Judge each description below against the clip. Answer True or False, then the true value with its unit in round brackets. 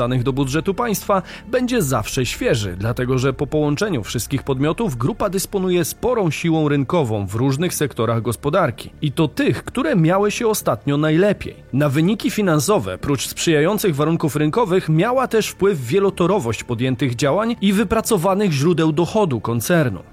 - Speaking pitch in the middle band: True (160 Hz)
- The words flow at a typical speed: True (140 wpm)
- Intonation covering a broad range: True (6.4 semitones)